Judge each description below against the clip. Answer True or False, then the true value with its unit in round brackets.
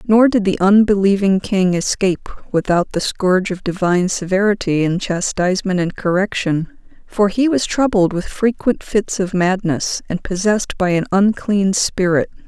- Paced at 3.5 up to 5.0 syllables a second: True (4.8 syllables/s)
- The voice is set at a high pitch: True (195 Hz)